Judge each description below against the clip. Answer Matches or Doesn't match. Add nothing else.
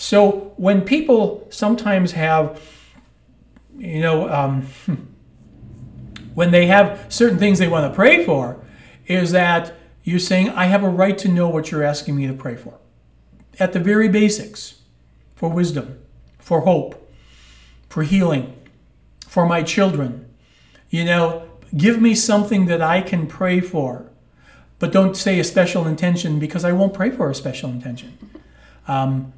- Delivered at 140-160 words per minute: Matches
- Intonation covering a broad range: Matches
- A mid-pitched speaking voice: Matches